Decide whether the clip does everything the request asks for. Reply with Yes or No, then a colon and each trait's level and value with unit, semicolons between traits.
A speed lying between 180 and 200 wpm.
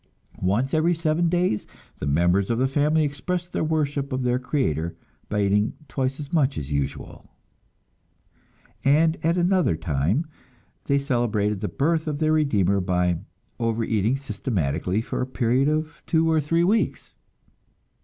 No: average, 145 wpm